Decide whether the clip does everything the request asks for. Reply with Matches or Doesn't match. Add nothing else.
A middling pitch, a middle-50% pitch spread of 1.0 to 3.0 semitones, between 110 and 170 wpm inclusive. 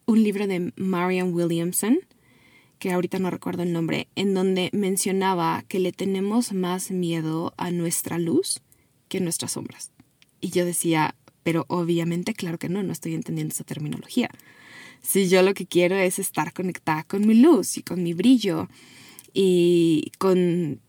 Matches